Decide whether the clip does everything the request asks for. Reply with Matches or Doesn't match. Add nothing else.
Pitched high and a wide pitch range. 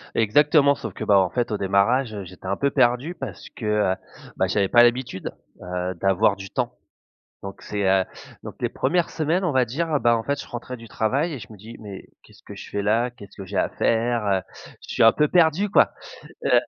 Doesn't match